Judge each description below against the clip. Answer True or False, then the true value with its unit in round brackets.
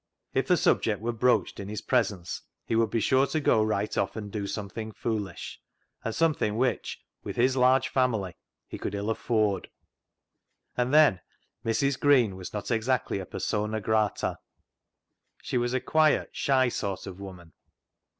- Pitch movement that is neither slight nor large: True (3.9 semitones)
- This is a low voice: True (110 Hz)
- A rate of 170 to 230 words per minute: False (160 wpm)